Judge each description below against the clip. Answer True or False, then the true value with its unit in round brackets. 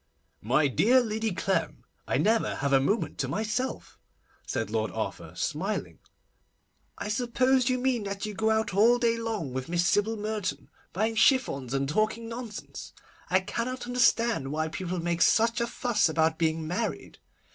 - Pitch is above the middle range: True (215 Hz)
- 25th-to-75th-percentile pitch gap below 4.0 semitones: False (5.6 semitones)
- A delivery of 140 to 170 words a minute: True (160 wpm)